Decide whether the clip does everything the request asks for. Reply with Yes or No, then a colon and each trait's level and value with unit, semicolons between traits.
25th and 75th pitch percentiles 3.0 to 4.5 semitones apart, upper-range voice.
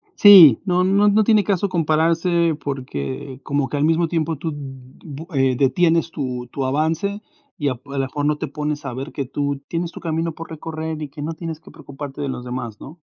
No: average, 3.3 semitones; medium, 155 Hz